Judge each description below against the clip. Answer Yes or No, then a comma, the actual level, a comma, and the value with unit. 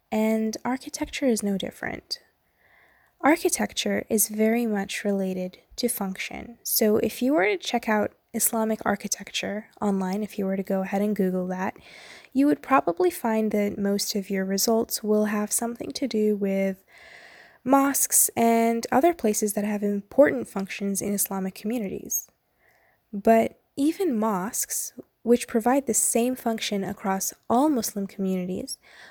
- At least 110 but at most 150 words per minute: Yes, average, 140 wpm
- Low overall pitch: No, high, 220 Hz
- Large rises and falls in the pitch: No, average, 3.3 semitones